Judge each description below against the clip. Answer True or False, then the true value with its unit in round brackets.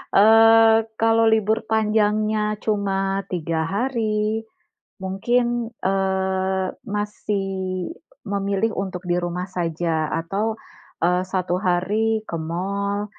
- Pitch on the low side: False (200 Hz)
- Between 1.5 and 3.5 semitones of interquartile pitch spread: True (2.8 semitones)